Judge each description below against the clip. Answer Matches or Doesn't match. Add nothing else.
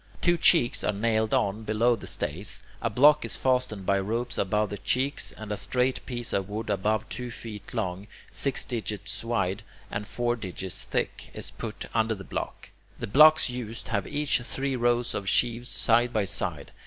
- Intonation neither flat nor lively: Matches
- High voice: Doesn't match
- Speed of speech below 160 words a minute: Doesn't match